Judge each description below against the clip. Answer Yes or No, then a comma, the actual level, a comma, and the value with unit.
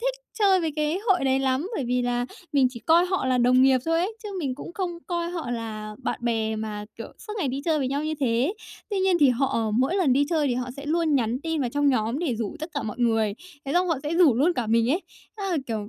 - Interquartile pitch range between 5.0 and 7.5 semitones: Yes, wide, 5.6 semitones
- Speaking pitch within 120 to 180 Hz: No, very high, 275 Hz